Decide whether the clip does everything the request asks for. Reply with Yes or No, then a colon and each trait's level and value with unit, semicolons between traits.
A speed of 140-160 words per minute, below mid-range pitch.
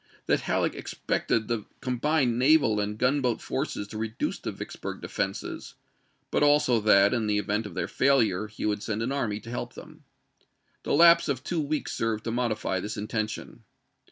No: average, 180 wpm; low, 115 Hz